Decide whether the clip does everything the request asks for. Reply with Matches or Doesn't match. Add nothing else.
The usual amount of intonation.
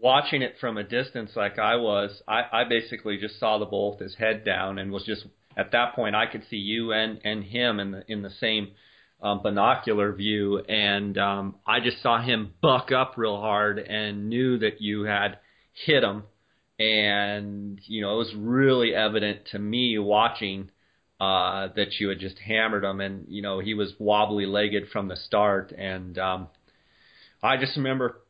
Doesn't match